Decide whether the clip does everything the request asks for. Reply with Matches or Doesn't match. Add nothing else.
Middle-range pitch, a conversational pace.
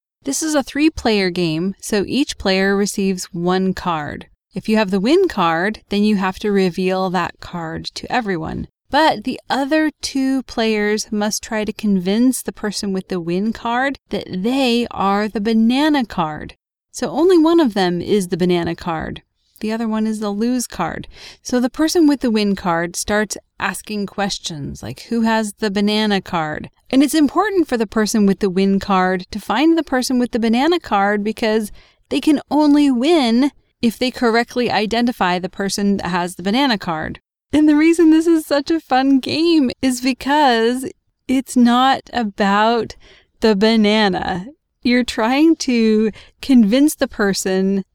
Doesn't match